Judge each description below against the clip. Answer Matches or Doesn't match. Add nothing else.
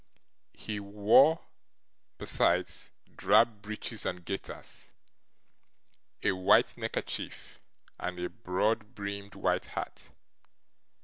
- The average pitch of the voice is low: Matches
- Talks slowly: Matches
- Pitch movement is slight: Matches